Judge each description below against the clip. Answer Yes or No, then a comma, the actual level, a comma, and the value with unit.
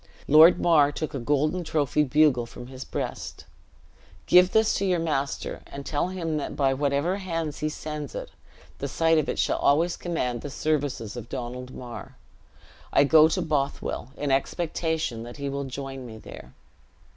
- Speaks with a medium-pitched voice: Yes, medium, 145 Hz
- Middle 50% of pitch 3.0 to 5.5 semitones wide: Yes, average, 3.3 semitones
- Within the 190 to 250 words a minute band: No, average, 170 wpm